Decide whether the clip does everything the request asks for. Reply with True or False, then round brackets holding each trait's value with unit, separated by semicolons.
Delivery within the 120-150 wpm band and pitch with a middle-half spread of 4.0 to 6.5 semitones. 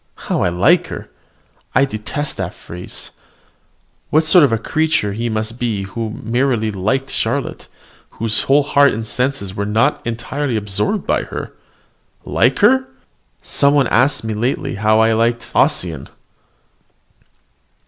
True (140 wpm; 4.8 semitones)